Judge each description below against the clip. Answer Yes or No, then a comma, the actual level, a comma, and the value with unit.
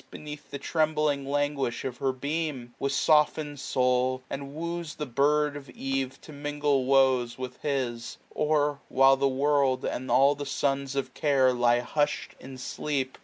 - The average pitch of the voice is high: No, medium, 140 Hz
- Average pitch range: No, narrow, 2.1 semitones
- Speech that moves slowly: No, average, 165 wpm